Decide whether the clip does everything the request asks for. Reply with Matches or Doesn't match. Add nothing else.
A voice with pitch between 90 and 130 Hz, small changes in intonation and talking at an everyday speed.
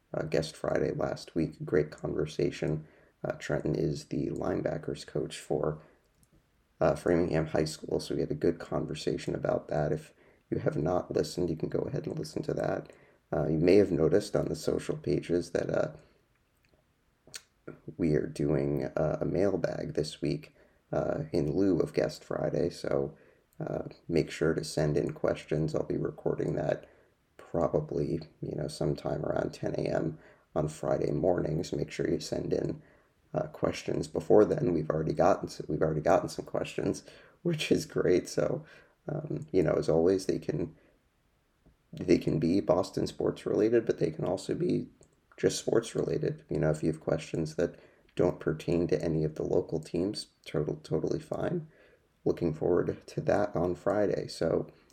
Doesn't match